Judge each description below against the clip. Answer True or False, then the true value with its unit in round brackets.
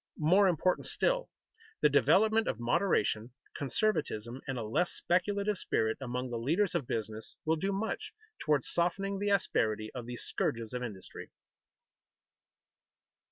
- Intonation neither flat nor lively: False (8.9 semitones)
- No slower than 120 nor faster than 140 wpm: True (135 wpm)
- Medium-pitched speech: True (150 Hz)